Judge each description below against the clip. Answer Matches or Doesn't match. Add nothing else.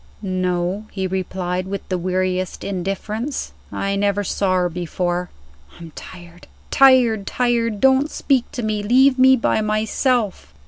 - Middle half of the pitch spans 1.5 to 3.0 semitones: Doesn't match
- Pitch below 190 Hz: Doesn't match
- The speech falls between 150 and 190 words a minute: Doesn't match